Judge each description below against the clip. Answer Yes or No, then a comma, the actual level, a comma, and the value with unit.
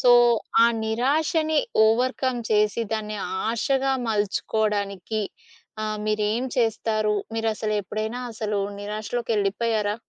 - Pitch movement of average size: No, narrow, 1.9 semitones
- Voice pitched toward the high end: Yes, high, 220 Hz